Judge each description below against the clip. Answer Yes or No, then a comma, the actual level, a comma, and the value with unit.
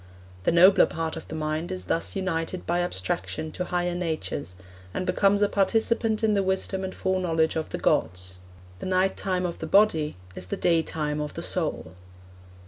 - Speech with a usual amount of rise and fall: Yes, average, 3.3 semitones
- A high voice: No, medium, 175 Hz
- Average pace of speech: Yes, average, 185 wpm